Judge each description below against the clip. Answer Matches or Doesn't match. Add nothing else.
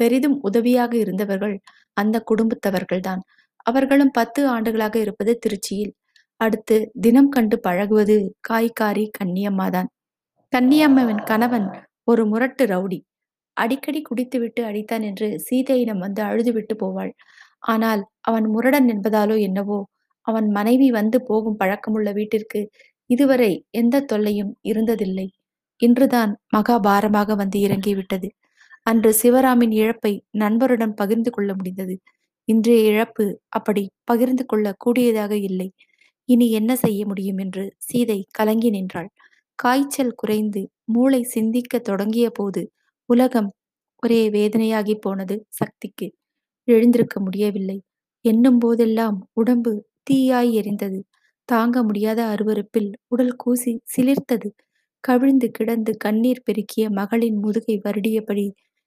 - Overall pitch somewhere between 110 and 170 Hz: Doesn't match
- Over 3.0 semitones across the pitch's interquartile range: Doesn't match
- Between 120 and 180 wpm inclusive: Doesn't match